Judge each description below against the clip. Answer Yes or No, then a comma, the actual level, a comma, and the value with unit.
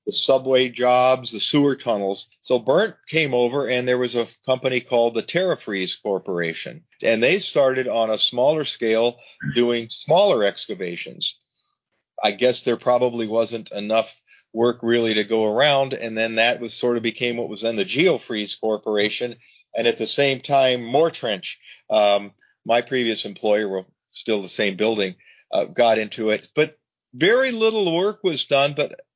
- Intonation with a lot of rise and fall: No, average, 2.8 semitones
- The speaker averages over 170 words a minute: No, average, 165 wpm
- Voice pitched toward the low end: Yes, low, 120 Hz